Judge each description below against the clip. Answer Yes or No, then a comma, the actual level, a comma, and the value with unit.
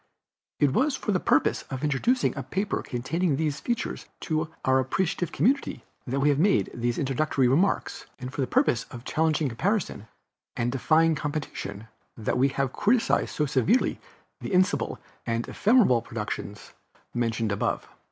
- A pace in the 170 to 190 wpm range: No, average, 150 wpm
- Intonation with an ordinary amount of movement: No, wide, 6.5 semitones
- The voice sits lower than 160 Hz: Yes, medium, 140 Hz